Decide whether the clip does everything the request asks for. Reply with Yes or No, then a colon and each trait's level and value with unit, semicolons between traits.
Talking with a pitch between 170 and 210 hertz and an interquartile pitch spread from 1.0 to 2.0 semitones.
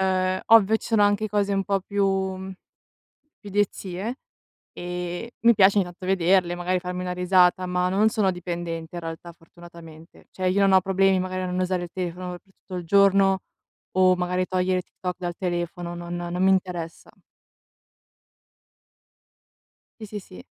Yes: medium, 185 Hz; narrow, 1.6 semitones